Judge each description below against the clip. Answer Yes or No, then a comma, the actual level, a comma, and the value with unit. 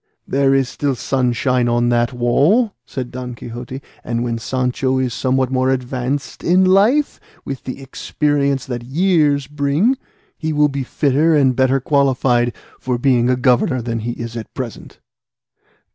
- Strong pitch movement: No, narrow, 2.6 semitones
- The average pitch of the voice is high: No, low, 130 Hz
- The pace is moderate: Yes, average, 155 wpm